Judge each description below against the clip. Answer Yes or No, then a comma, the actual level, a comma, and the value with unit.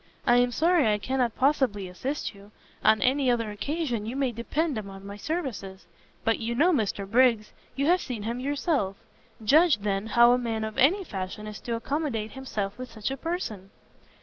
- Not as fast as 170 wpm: No, average, 185 wpm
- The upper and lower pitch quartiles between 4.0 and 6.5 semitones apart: Yes, average, 4.8 semitones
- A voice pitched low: No, high, 235 Hz